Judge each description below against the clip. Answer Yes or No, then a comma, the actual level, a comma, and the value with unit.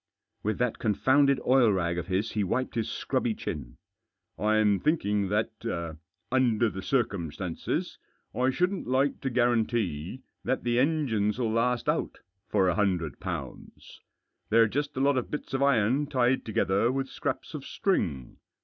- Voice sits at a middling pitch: No, low, 115 Hz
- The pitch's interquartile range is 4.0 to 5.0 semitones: Yes, average, 4.4 semitones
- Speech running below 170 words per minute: Yes, average, 155 wpm